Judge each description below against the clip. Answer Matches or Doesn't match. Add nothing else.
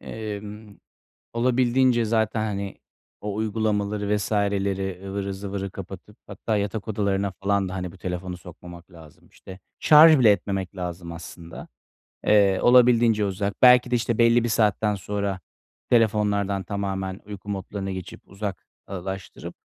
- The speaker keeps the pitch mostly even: Matches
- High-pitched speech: Doesn't match